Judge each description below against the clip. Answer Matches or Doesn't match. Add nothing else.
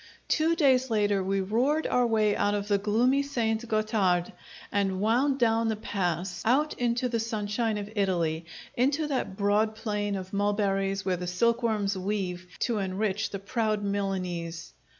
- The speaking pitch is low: Doesn't match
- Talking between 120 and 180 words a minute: Matches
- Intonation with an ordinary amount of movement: Matches